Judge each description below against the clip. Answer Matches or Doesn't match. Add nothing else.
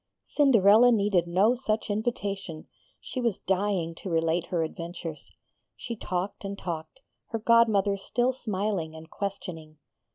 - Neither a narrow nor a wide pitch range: Matches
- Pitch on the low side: Doesn't match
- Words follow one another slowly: Matches